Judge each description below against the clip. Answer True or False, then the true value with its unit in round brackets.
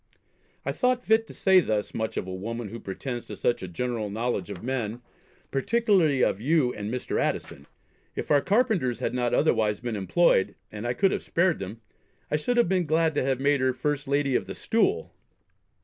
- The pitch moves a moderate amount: False (7.0 semitones)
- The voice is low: True (130 Hz)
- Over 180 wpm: True (200 wpm)